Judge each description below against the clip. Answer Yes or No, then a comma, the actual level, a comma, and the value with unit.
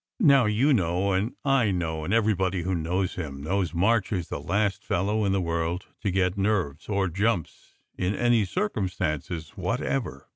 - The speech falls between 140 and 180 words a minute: Yes, average, 175 wpm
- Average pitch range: Yes, average, 3.9 semitones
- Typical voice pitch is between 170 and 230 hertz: No, very low, 95 Hz